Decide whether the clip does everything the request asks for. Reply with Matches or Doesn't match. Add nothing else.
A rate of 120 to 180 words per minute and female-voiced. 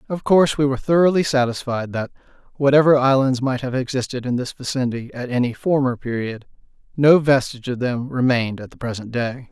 Doesn't match